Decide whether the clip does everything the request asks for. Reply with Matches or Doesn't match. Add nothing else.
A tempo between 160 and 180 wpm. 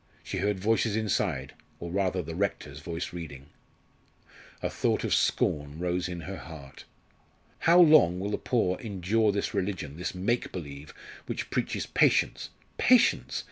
Doesn't match